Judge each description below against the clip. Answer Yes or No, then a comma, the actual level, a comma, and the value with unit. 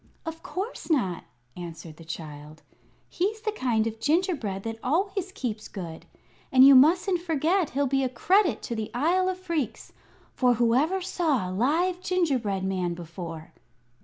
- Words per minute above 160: No, average, 155 wpm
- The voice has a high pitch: Yes, very high, 265 Hz